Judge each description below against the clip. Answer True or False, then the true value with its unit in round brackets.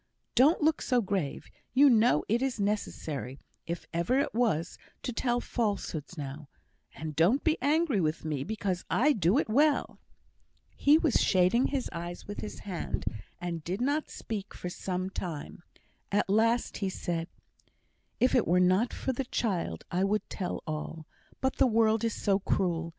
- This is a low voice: False (200 Hz)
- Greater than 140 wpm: True (165 wpm)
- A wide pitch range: True (6.2 semitones)